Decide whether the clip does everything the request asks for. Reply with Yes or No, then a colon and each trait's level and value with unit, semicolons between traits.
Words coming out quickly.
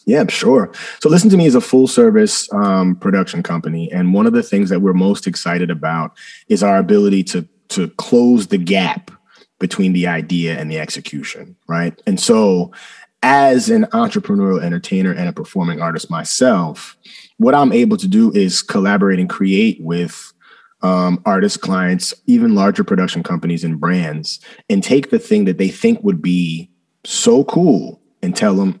No: average, 170 wpm